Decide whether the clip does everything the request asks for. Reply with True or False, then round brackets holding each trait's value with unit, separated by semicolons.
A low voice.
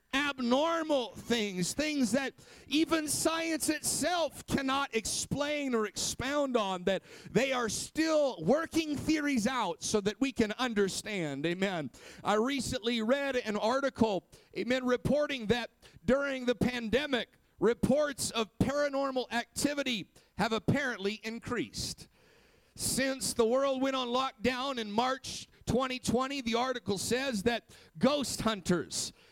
False (250 Hz)